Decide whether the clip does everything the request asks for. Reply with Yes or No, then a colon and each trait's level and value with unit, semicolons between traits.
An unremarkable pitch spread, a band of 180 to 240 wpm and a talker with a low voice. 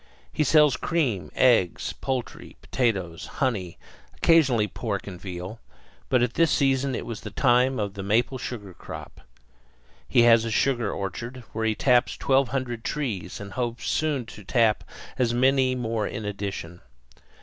No: average, 4.2 semitones; average, 155 wpm; low, 120 Hz